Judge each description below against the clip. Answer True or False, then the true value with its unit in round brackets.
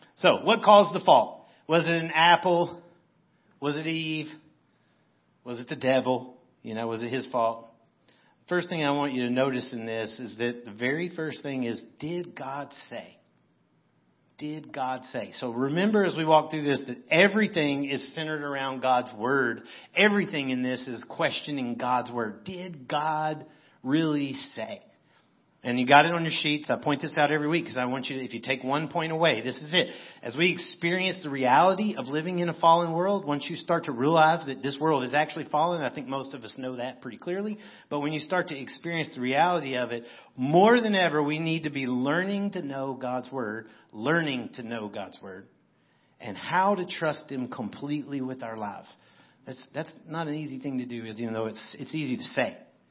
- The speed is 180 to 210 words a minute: True (200 wpm)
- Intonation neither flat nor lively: True (4.6 semitones)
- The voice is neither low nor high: True (145 Hz)